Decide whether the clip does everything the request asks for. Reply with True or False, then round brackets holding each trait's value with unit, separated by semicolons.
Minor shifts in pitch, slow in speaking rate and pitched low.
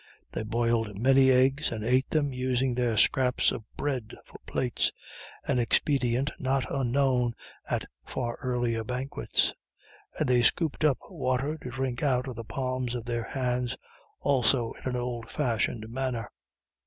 False (2.0 semitones; 150 wpm; 125 Hz)